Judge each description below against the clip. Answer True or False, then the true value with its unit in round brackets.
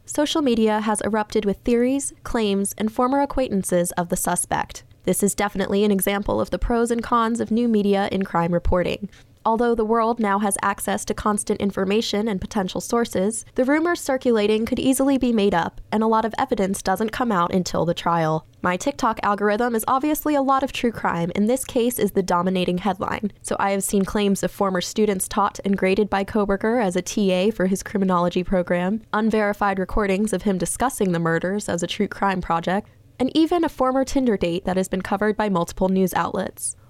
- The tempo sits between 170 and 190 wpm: False (200 wpm)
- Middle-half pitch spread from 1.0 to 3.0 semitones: False (3.7 semitones)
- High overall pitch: True (205 Hz)